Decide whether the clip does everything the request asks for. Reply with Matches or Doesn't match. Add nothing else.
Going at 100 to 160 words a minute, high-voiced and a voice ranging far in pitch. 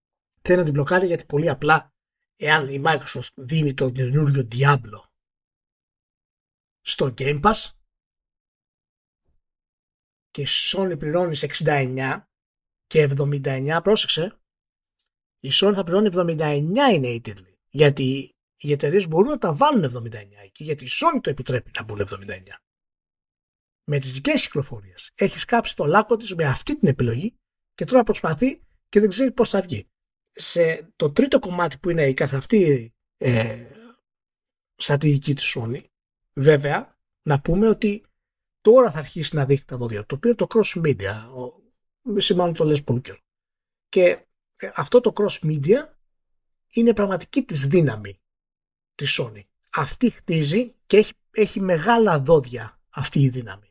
Doesn't match